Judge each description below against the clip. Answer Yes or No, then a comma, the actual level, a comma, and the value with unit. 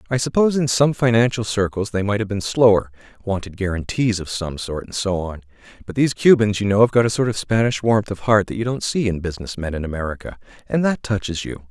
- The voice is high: No, low, 105 Hz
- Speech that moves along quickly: Yes, fast, 235 wpm